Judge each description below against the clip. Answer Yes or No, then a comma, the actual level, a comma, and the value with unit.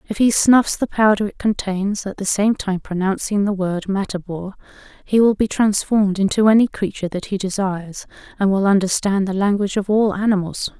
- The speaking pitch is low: No, high, 200 Hz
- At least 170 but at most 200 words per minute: Yes, average, 185 wpm